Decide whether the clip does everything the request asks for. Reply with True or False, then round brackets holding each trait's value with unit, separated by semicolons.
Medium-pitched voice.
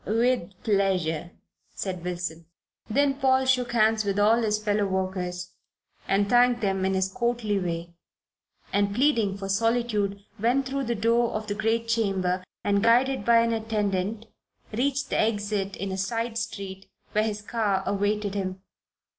False (210 Hz)